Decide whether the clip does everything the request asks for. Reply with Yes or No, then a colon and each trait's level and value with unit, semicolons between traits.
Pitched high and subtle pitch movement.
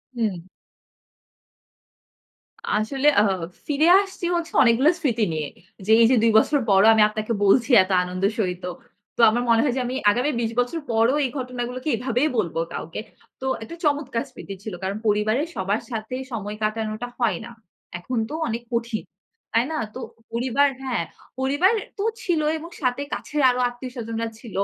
No: high, 235 Hz; average, 3.6 semitones